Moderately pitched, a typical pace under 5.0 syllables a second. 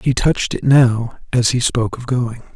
No: low, 120 Hz; 4.8 syllables/s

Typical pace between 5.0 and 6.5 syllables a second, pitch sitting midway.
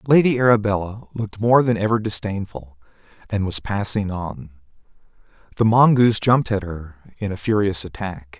No: 5.3 syllables/s; low, 100 Hz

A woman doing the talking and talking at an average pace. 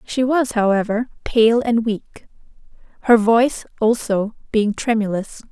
No: female; slow, 120 wpm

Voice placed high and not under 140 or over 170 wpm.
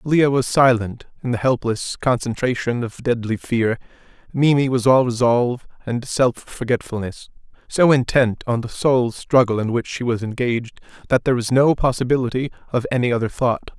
No: low, 125 Hz; average, 160 wpm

